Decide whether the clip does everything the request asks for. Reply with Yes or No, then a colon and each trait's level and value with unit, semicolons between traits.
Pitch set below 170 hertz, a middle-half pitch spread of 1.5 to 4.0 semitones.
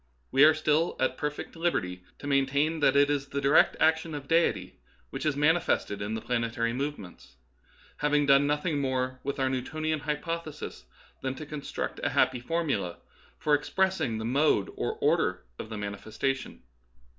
Yes: medium, 140 Hz; average, 3.4 semitones